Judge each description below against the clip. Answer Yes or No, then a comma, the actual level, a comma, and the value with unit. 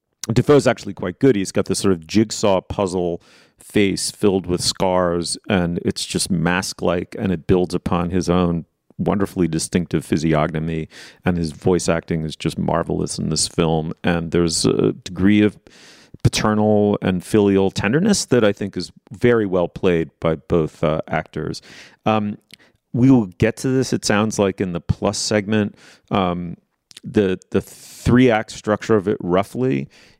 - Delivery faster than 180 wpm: No, average, 160 wpm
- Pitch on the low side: Yes, very low, 95 Hz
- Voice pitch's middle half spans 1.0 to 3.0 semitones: No, average, 3.7 semitones